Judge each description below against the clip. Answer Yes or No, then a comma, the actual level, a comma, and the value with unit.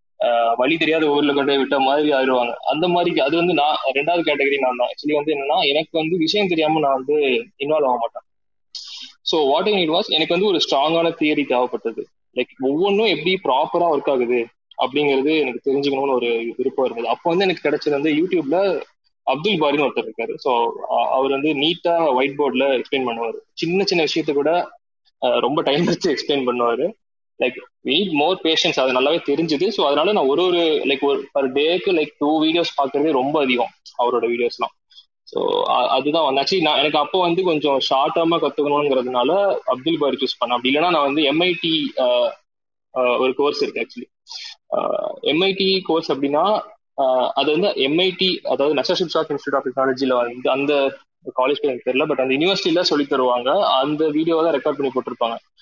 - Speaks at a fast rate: Yes, fast, 160 wpm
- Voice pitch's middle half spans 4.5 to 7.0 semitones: Yes, average, 4.9 semitones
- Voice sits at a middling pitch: Yes, medium, 155 Hz